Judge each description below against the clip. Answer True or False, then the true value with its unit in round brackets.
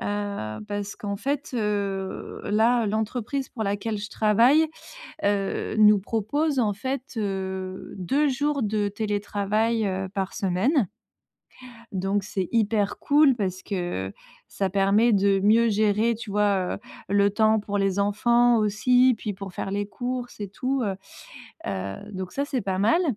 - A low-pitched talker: False (205 Hz)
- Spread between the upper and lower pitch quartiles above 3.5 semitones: False (3.0 semitones)